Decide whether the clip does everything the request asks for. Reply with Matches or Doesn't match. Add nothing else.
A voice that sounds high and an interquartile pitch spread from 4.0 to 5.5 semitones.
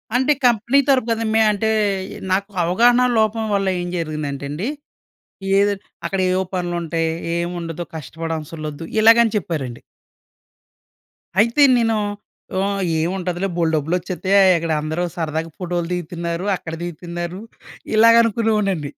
Doesn't match